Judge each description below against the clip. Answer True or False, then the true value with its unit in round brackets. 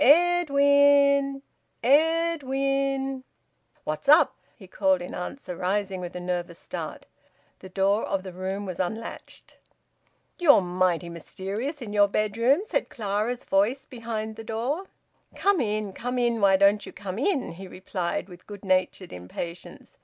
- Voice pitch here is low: False (215 Hz)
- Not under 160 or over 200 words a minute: False (145 wpm)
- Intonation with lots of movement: True (6.5 semitones)